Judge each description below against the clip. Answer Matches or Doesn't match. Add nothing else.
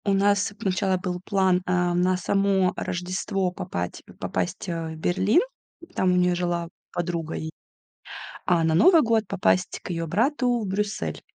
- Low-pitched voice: Doesn't match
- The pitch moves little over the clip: Matches